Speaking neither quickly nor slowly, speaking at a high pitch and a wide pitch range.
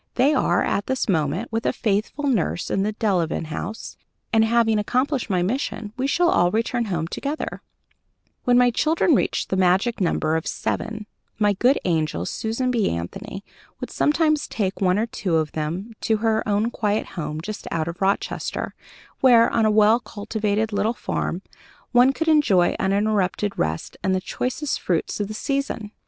No: average, 175 wpm; high, 215 Hz; average, 4.3 semitones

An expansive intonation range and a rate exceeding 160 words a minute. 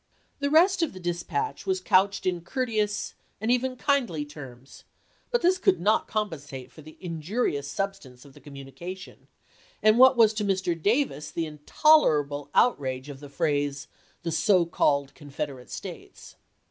No: wide, 8.0 semitones; average, 155 wpm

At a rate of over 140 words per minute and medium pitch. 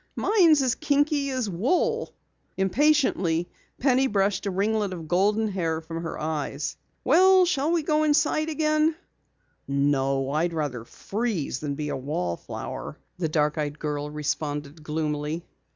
No: slow, 135 wpm; medium, 180 Hz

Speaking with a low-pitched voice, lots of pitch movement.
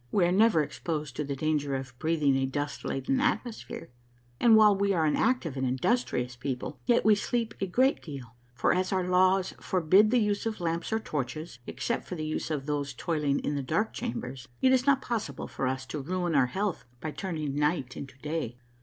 No: medium, 160 Hz; wide, 6.5 semitones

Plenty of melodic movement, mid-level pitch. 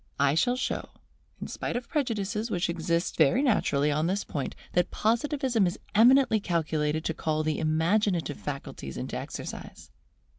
Yes: wide, 6.5 semitones; medium, 175 Hz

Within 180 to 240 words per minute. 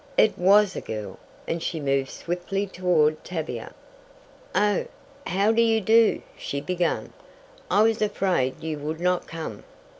No: average, 145 wpm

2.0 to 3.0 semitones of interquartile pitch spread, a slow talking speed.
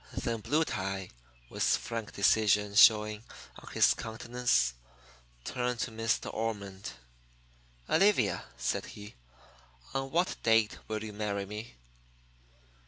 Yes: narrow, 2.4 semitones; slow, 115 wpm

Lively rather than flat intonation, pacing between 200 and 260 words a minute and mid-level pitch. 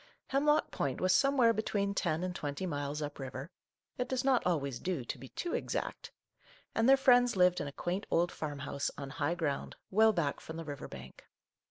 Yes: wide, 7.9 semitones; fast, 205 wpm; medium, 175 Hz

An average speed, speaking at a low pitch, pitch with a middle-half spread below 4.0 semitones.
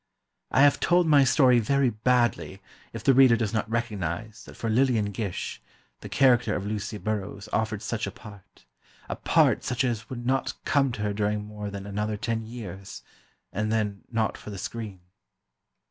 Yes: average, 175 wpm; low, 110 Hz; average, 2.9 semitones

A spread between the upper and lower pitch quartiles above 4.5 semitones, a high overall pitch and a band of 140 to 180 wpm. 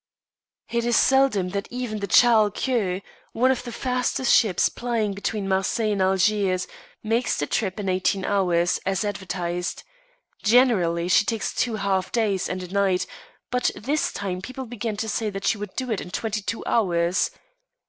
No: average, 3.7 semitones; high, 205 Hz; average, 170 wpm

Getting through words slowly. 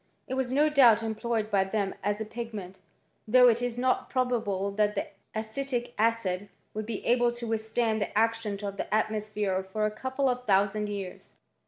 No: average, 180 wpm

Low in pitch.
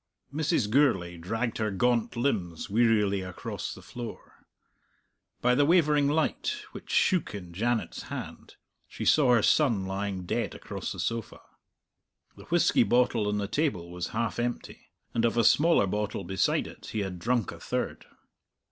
Yes: low, 115 Hz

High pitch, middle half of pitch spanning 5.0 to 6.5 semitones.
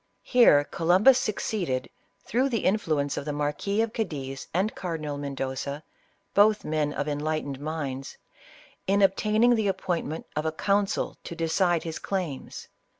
No: medium, 165 Hz; wide, 5.6 semitones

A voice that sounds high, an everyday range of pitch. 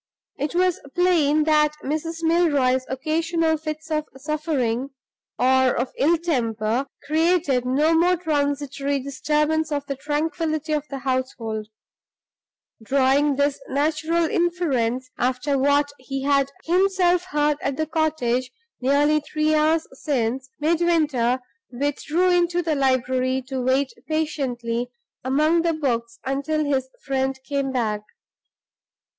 Yes: very high, 285 Hz; average, 3.2 semitones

